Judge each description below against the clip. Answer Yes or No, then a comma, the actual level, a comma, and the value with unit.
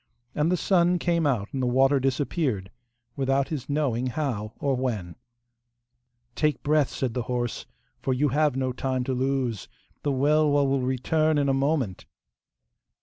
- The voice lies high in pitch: No, low, 135 Hz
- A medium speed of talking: Yes, average, 155 wpm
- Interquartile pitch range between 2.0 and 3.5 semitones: Yes, average, 2.9 semitones